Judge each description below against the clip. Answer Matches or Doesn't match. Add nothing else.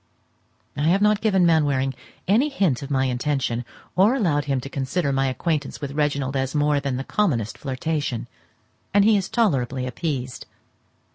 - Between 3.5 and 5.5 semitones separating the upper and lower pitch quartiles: Matches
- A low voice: Doesn't match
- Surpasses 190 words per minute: Doesn't match